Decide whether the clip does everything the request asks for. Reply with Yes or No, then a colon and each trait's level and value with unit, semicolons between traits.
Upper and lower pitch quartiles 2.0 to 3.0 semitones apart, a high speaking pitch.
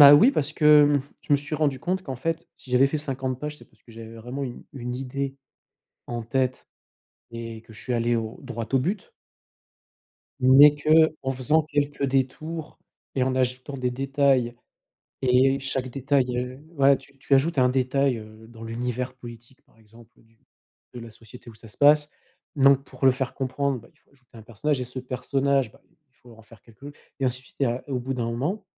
No: narrow, 2.6 semitones; low, 130 Hz